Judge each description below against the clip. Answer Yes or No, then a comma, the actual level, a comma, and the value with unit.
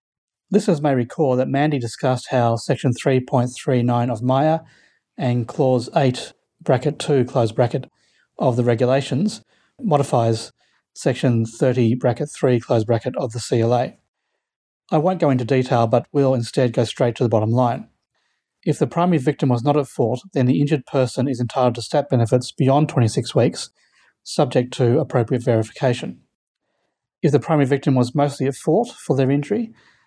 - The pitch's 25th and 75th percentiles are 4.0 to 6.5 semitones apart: No, average, 2.9 semitones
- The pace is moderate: Yes, average, 160 wpm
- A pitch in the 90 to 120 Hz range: No, low, 130 Hz